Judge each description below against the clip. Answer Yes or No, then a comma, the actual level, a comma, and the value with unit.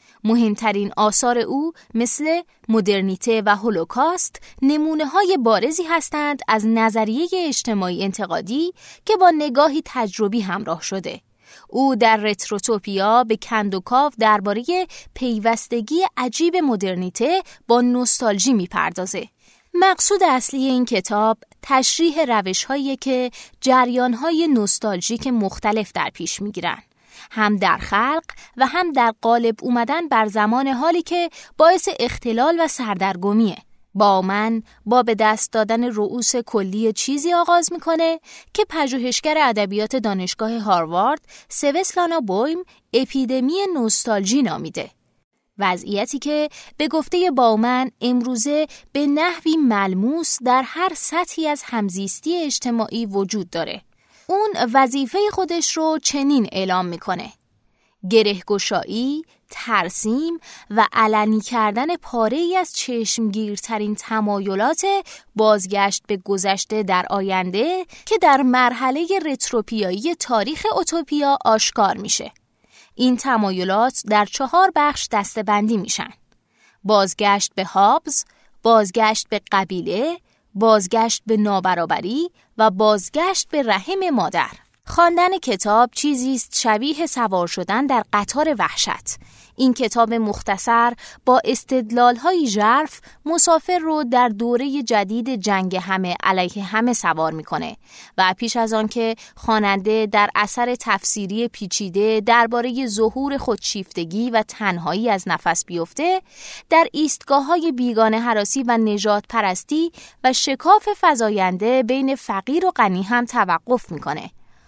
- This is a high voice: Yes, high, 235 Hz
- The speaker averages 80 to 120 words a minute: Yes, average, 110 wpm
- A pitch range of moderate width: No, wide, 5.9 semitones